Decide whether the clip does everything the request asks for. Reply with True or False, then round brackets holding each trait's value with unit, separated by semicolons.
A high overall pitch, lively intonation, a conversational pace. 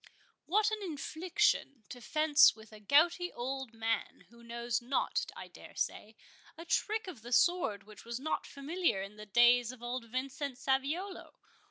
True (260 Hz; 5.7 semitones; 160 wpm)